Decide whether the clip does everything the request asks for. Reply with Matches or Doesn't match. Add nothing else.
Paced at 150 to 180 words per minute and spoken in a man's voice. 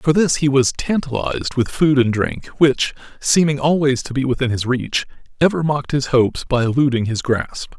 Doesn't match